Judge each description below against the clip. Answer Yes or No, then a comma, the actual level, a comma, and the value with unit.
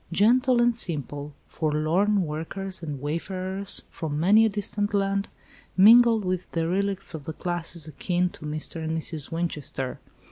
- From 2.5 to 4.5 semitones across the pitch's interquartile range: Yes, average, 4.2 semitones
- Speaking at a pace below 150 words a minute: Yes, average, 140 wpm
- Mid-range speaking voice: Yes, medium, 175 Hz